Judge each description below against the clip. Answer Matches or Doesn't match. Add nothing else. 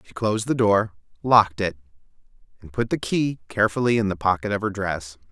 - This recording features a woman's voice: Doesn't match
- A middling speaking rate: Matches